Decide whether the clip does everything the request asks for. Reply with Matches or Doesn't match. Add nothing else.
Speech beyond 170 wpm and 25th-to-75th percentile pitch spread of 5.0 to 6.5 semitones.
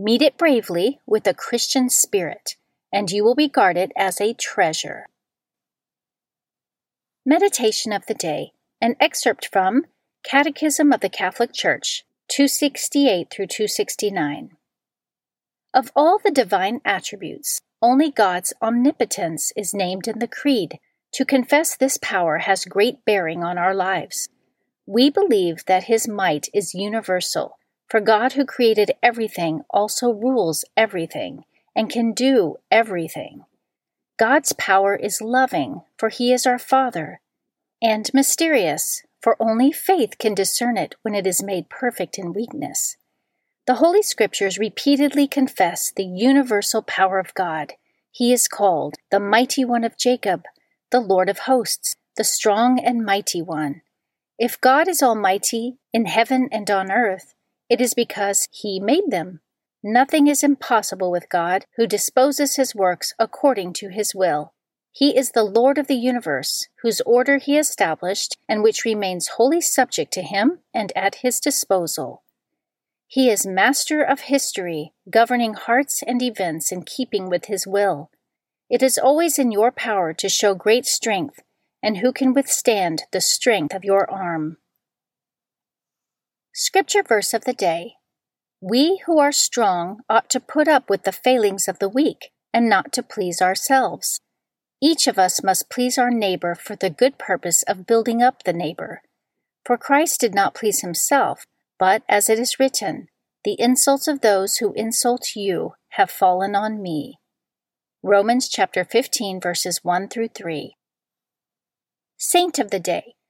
Doesn't match